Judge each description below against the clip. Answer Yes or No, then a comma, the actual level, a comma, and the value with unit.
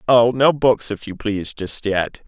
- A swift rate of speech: Yes, fast, 210 wpm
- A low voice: Yes, low, 110 Hz